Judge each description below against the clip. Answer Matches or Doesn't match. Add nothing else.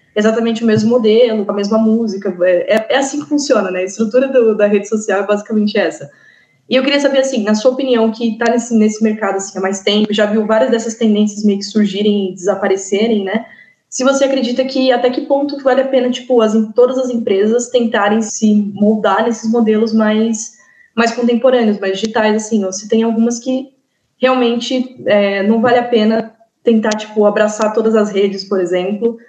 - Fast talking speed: Matches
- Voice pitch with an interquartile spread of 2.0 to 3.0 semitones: Matches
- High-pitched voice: Matches